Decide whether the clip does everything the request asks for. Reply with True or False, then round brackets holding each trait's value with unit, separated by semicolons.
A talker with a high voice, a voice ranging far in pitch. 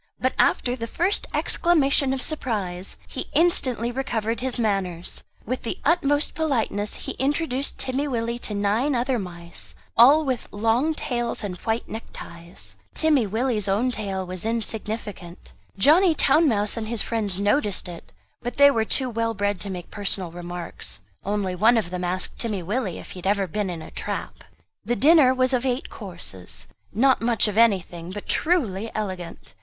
False (225 Hz; 5.0 semitones)